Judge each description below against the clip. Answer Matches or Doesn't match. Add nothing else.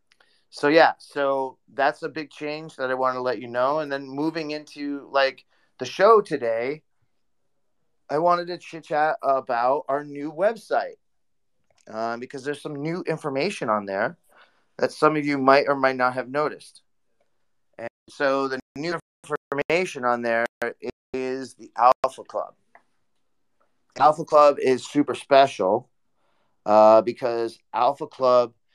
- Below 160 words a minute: Matches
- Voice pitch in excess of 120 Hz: Matches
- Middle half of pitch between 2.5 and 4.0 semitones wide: Matches